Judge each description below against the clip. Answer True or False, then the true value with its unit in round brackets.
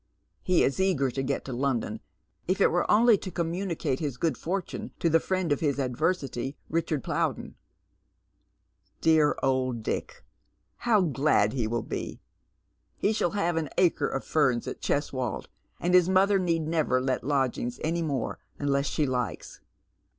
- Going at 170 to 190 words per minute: False (160 wpm)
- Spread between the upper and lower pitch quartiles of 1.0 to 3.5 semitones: False (5.1 semitones)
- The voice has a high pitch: False (150 Hz)